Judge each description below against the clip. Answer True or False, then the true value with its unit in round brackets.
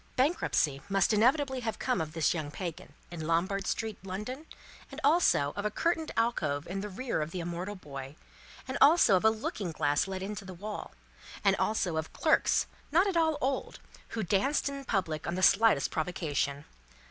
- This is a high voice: True (195 Hz)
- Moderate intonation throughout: False (7.5 semitones)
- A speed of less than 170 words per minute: False (180 wpm)